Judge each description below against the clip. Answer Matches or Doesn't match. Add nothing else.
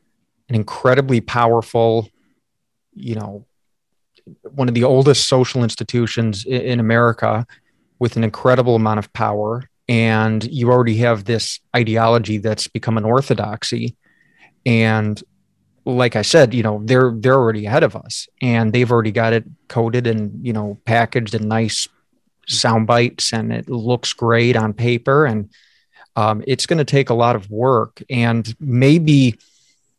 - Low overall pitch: Matches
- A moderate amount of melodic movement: Doesn't match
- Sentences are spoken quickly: Doesn't match